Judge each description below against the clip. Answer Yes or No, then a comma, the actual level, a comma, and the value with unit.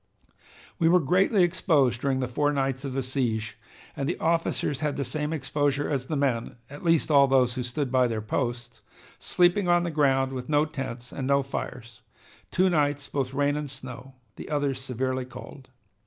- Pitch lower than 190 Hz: Yes, low, 135 Hz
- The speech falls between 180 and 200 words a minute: Yes, average, 185 wpm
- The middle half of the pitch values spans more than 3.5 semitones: No, average, 2.7 semitones